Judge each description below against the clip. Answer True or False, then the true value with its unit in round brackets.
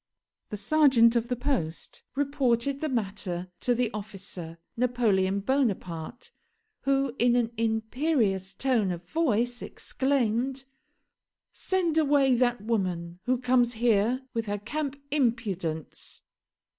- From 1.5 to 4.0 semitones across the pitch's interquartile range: False (4.8 semitones)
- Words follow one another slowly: True (115 wpm)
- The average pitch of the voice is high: True (235 Hz)